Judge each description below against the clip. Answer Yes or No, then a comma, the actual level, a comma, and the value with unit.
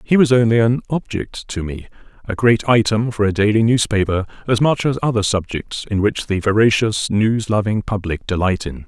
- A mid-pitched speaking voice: No, low, 110 Hz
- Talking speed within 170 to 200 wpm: Yes, average, 185 wpm